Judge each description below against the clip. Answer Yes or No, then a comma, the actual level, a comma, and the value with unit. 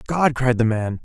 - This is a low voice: Yes, low, 125 Hz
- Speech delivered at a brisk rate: Yes, fast, 230 wpm